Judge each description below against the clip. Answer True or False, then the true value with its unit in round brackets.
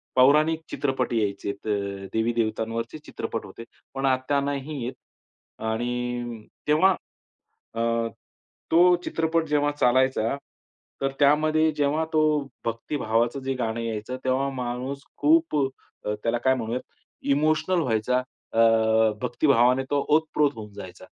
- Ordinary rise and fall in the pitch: True (4.2 semitones)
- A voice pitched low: True (130 Hz)